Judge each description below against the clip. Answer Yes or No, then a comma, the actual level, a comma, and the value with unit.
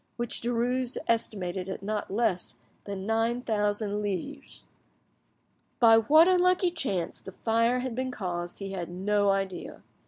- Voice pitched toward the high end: Yes, high, 215 Hz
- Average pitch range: Yes, average, 4.1 semitones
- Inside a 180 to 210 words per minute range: No, slow, 135 wpm